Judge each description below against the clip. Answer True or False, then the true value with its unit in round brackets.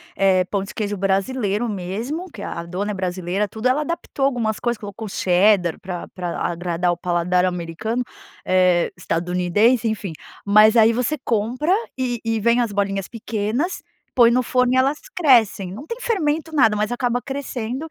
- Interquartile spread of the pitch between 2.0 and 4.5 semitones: False (5.1 semitones)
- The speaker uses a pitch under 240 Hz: True (215 Hz)